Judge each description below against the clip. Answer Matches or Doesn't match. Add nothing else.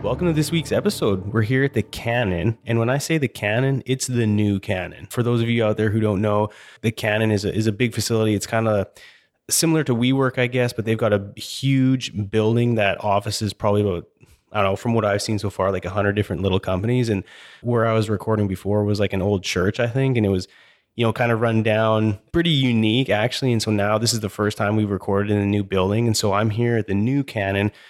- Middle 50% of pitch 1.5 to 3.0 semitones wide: Matches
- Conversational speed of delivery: Doesn't match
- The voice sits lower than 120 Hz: Matches